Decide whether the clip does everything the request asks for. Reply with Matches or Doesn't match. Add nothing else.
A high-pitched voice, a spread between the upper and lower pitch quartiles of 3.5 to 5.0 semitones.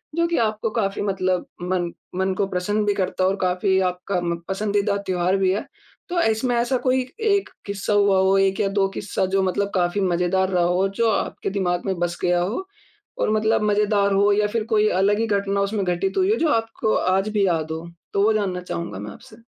Doesn't match